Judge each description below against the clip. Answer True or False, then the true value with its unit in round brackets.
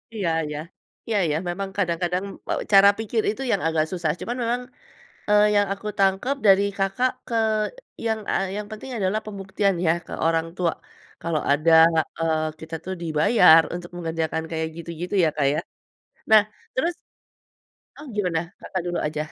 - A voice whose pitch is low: False (185 Hz)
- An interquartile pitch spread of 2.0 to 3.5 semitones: False (4.1 semitones)